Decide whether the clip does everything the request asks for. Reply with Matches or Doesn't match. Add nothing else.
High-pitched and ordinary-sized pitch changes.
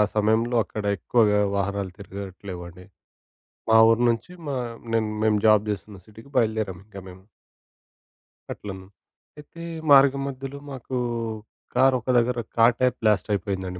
Doesn't match